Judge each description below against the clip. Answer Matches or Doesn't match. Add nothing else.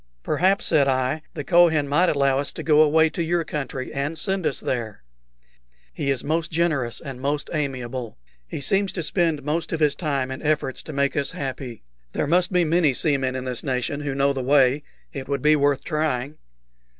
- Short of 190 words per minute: Doesn't match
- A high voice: Doesn't match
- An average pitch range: Matches